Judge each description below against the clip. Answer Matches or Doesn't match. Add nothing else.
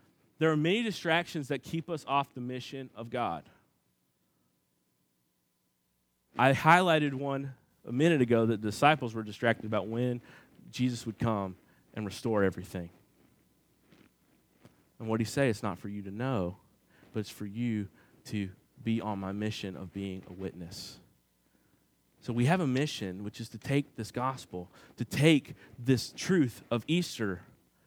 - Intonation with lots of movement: Matches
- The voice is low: Matches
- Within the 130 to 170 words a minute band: Matches